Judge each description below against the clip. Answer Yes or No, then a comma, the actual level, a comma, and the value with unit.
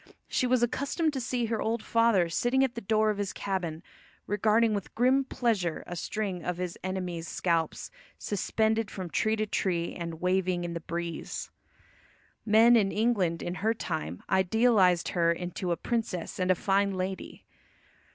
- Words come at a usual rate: Yes, average, 160 wpm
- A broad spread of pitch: No, average, 4.3 semitones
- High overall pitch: Yes, high, 195 Hz